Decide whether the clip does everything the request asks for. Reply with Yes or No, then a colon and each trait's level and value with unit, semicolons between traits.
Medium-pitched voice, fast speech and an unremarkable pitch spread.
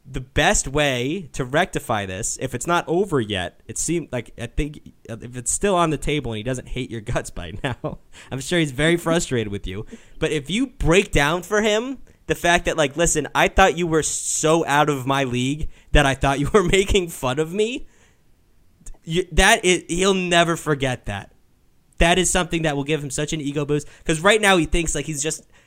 Yes: medium, 150 Hz; fast, 215 wpm; average, 4.7 semitones